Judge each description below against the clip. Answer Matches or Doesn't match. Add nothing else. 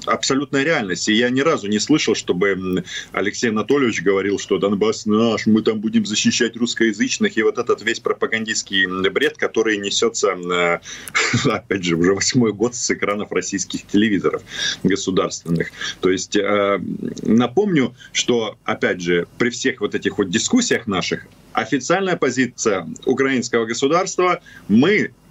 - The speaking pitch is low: Matches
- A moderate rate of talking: Matches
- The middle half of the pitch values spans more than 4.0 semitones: Matches